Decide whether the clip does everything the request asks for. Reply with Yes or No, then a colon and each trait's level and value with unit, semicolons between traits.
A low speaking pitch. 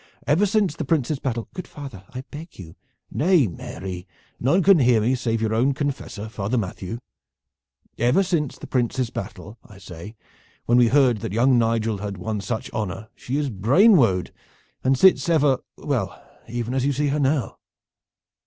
Yes: low, 120 Hz